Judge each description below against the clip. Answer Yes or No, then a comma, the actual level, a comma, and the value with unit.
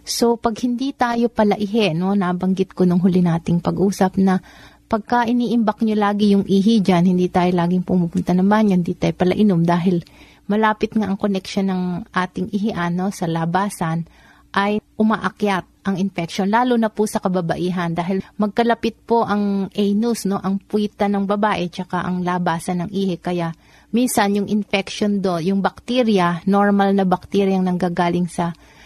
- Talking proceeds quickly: Yes, fast, 160 wpm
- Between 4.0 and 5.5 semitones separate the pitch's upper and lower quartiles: No, average, 2.8 semitones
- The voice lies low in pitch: No, high, 195 Hz